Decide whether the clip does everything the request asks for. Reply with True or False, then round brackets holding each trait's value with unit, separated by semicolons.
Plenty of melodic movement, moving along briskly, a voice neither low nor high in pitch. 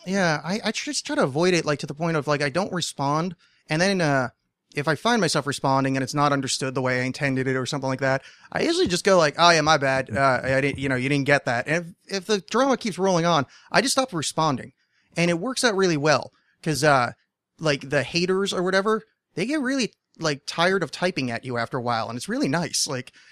True (5.7 semitones; 250 wpm; 155 Hz)